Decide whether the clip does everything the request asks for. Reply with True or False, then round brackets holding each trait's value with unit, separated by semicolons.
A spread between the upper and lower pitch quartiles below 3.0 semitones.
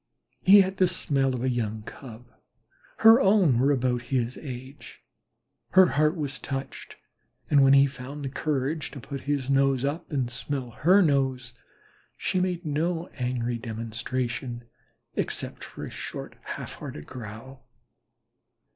False (3.5 semitones)